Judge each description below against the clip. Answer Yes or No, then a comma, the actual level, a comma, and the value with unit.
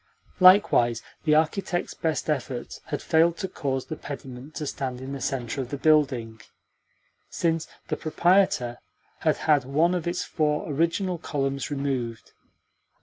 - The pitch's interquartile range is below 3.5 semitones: No, average, 3.9 semitones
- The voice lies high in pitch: No, medium, 145 Hz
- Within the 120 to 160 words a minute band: Yes, average, 145 wpm